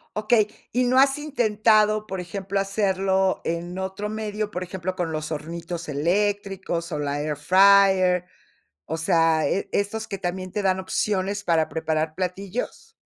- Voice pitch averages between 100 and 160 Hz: No, high, 190 Hz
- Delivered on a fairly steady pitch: No, average, 3.5 semitones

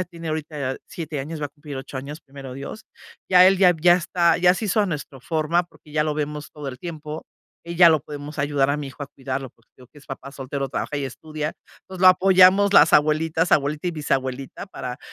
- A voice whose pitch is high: No, medium, 150 Hz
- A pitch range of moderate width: Yes, average, 3.7 semitones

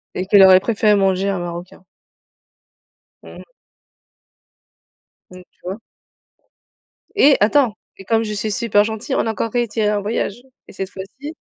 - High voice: Yes, high, 210 Hz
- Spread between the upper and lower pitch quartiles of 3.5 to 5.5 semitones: No, average, 2.9 semitones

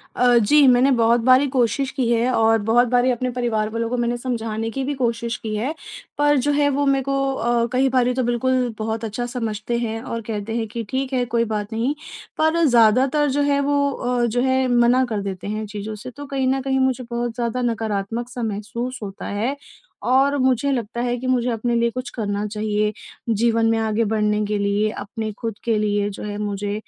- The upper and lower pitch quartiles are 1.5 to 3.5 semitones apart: Yes, average, 2.8 semitones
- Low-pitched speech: No, high, 235 Hz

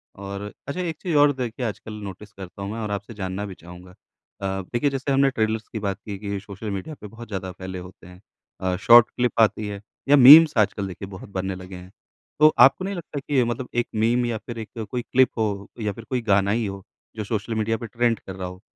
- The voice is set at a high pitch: No, low, 105 Hz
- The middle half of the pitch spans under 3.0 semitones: No, average, 3.7 semitones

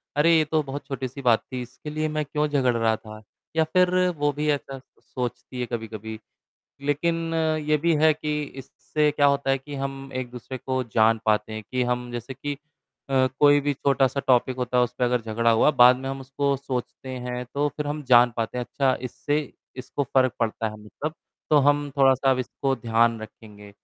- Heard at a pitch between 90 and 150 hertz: Yes, low, 135 Hz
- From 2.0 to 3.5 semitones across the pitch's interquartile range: Yes, average, 3.2 semitones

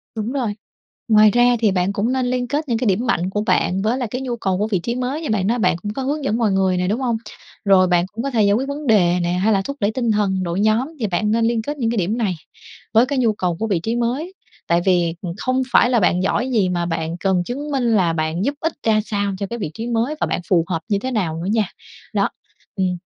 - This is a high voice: Yes, high, 215 Hz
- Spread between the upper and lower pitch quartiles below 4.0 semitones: No, average, 4.6 semitones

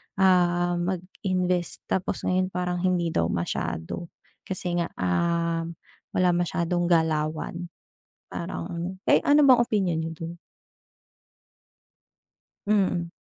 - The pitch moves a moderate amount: No, narrow, 1.5 semitones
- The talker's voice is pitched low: No, medium, 175 Hz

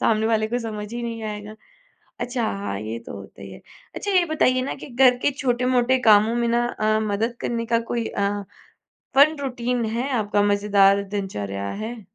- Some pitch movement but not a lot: Yes, average, 3.1 semitones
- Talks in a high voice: Yes, high, 225 Hz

